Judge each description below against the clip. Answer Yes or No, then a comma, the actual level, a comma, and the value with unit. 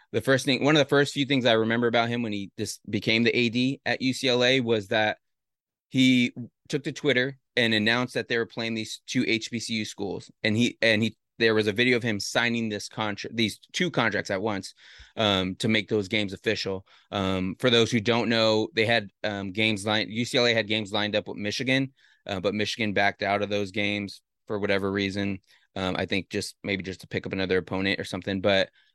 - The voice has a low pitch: Yes, low, 110 Hz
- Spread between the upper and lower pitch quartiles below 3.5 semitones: Yes, average, 2.9 semitones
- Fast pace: Yes, fast, 215 wpm